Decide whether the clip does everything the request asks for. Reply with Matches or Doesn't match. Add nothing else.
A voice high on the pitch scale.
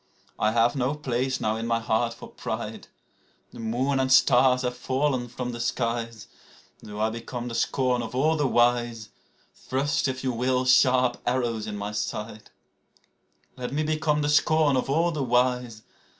Doesn't match